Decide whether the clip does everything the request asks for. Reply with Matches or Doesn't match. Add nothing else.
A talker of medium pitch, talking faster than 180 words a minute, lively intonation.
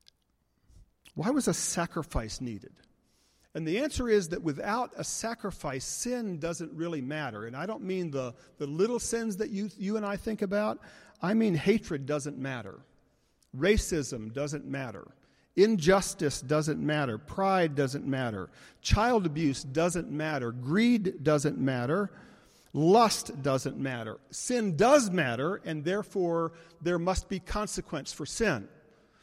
Doesn't match